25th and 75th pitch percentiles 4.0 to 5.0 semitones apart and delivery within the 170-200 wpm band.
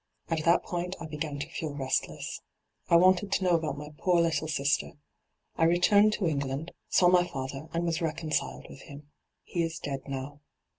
No: average, 3.3 semitones; average, 185 wpm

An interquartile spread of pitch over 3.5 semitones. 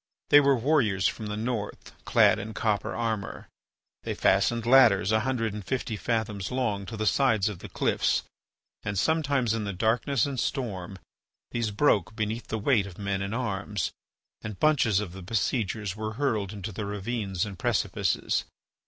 No: average, 3.1 semitones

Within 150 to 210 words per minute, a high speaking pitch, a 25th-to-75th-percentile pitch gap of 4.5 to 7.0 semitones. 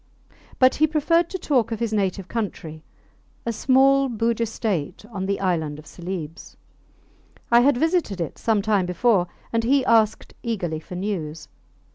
Yes: average, 155 wpm; high, 215 Hz; wide, 5.6 semitones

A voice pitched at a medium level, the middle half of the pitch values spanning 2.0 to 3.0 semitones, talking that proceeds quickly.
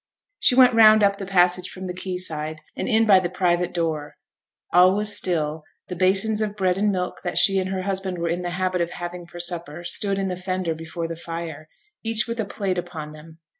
Yes: medium, 180 Hz; narrow, 2.4 semitones; fast, 225 wpm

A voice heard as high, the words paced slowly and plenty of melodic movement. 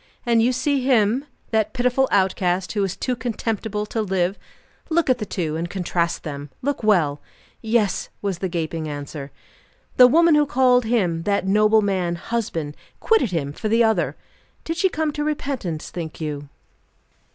No: high, 210 Hz; average, 165 wpm; wide, 6.4 semitones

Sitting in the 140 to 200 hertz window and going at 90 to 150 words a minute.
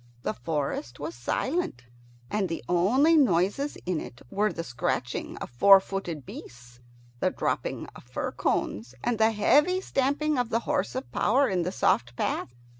No: high, 190 Hz; average, 165 wpm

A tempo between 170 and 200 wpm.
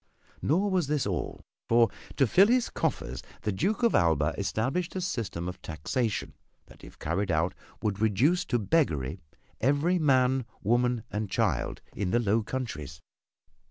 No: average, 155 wpm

